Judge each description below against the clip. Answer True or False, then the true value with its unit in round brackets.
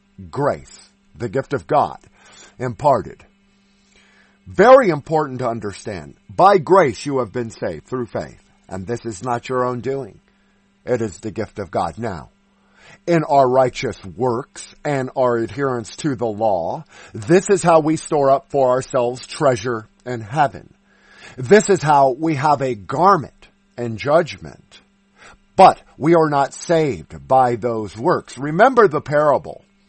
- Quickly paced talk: False (145 wpm)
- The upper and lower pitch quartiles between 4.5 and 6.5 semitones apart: True (5.4 semitones)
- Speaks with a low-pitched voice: True (130 Hz)